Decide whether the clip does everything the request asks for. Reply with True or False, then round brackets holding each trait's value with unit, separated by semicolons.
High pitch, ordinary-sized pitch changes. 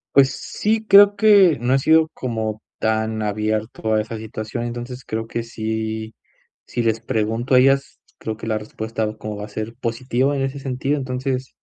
False (115 Hz; 3.4 semitones)